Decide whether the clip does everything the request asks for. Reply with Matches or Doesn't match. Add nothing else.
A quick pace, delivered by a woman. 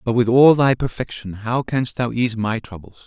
Doesn't match